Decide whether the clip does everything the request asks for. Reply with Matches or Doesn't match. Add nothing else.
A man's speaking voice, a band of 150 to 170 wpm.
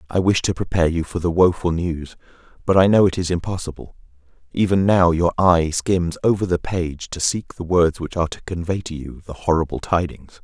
Doesn't match